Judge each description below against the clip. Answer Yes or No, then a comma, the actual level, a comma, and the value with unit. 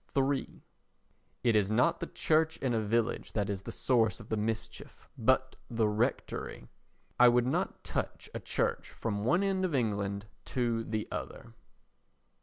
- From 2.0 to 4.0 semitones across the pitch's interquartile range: Yes, average, 3.5 semitones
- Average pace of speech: Yes, average, 160 wpm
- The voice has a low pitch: Yes, low, 115 Hz